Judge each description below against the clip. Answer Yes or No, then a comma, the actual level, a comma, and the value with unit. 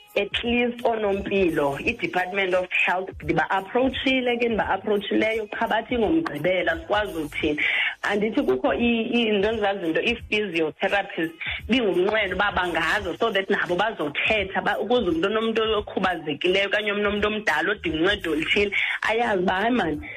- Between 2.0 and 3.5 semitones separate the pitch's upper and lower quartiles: No, average, 4.0 semitones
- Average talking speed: No, slow, 115 wpm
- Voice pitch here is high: Yes, high, 205 Hz